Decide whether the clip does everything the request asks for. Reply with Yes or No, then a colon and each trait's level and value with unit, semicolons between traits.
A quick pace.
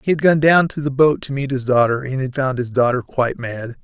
Yes: fast, 280 wpm